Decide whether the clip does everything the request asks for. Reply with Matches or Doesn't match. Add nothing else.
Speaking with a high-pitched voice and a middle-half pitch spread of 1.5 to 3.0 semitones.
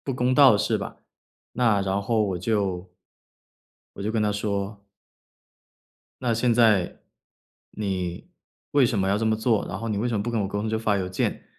Doesn't match